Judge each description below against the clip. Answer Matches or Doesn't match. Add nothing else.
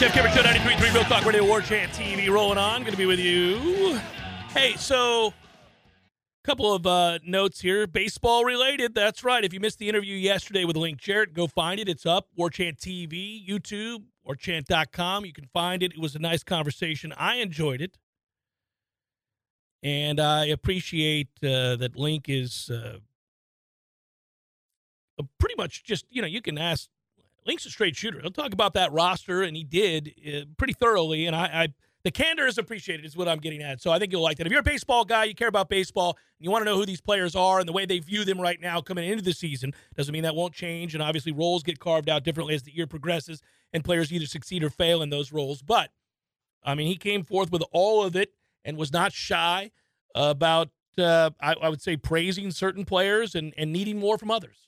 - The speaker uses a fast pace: Matches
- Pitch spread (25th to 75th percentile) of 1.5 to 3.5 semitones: Doesn't match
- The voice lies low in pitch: Doesn't match